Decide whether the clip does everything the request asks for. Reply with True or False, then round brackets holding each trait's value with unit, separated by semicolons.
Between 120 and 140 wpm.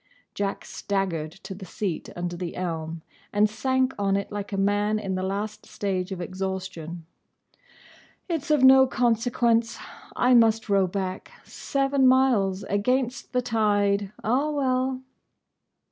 True (135 wpm)